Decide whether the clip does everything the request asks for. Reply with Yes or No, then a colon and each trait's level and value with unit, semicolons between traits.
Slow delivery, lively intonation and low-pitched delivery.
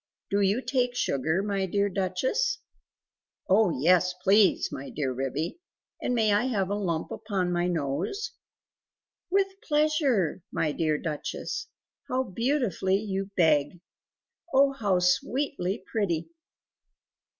No: slow, 120 wpm; wide, 6.1 semitones; high, 195 Hz